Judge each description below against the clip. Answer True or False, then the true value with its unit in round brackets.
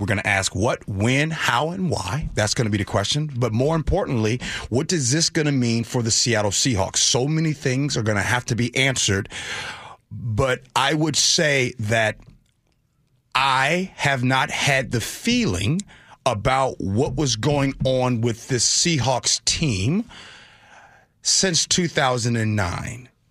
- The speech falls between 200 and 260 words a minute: False (155 wpm)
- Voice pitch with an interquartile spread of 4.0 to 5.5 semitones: True (4.5 semitones)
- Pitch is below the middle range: True (130 Hz)